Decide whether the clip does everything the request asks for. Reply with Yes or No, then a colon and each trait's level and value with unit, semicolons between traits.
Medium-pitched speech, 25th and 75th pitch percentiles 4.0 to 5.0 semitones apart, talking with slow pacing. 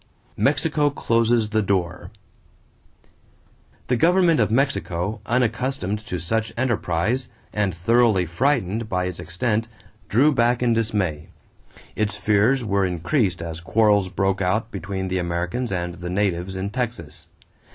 No: low, 105 Hz; average, 4.5 semitones; slow, 130 wpm